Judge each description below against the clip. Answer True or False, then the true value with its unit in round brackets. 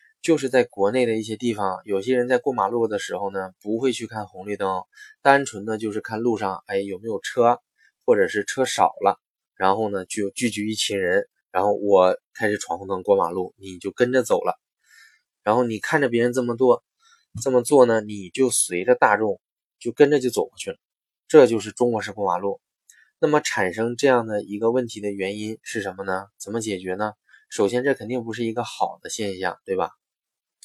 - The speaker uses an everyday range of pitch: True (4.0 semitones)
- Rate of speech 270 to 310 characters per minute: True (290 characters per minute)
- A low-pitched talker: True (115 Hz)